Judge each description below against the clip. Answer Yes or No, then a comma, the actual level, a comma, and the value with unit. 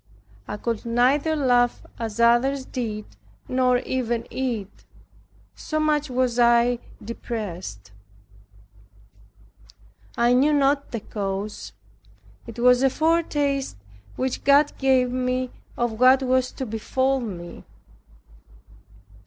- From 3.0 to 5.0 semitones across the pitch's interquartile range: No, narrow, 2.5 semitones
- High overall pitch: Yes, very high, 250 Hz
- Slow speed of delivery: Yes, slow, 105 wpm